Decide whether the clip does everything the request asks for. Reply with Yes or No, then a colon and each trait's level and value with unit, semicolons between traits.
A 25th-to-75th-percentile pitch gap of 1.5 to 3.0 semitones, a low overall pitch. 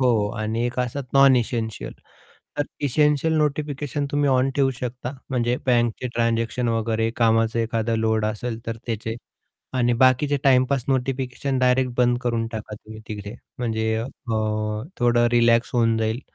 Yes: narrow, 2.4 semitones; low, 120 Hz